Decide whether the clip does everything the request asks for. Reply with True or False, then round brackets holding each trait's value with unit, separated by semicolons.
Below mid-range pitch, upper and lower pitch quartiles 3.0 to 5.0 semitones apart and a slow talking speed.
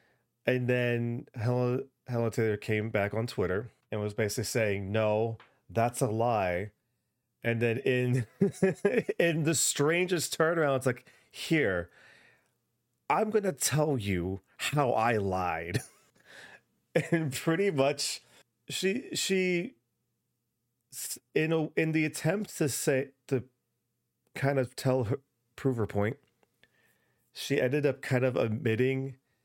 True (125 Hz; 3.6 semitones; 120 wpm)